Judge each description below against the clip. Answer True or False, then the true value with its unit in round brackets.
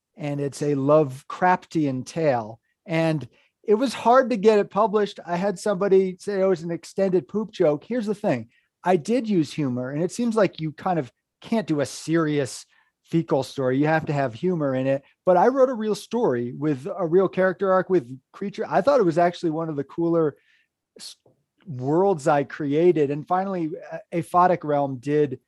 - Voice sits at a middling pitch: True (170 Hz)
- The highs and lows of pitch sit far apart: False (5.0 semitones)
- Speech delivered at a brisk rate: False (190 wpm)